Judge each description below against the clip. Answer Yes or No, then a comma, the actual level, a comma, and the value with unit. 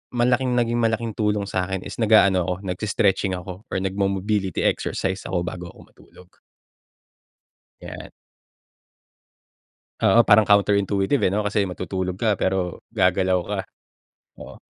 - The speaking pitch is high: No, low, 100 Hz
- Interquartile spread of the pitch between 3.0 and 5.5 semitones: No, narrow, 2.5 semitones